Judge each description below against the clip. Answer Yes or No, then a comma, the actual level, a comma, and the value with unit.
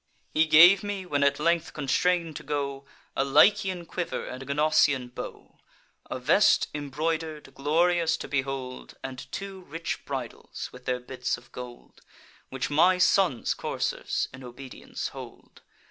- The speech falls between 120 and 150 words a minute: Yes, average, 145 wpm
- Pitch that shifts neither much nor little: Yes, average, 4.2 semitones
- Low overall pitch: No, medium, 150 Hz